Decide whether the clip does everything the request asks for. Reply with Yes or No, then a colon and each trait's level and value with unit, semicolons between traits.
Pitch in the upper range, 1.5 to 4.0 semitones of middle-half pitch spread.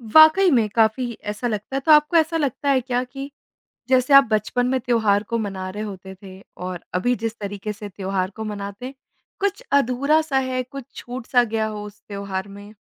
No: high, 230 Hz; average, 4.7 semitones